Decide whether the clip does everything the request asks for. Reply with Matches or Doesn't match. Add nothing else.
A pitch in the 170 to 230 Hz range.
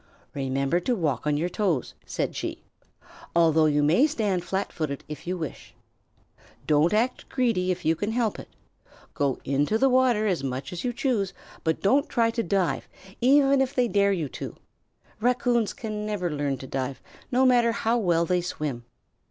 Matches